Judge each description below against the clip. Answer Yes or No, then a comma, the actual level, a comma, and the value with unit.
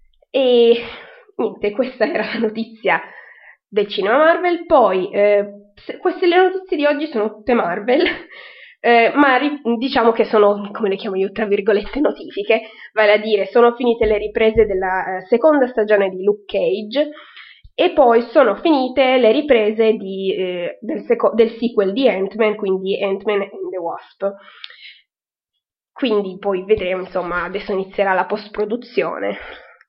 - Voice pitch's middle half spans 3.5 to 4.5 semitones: Yes, average, 4.2 semitones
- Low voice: No, high, 220 Hz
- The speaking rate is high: No, average, 145 wpm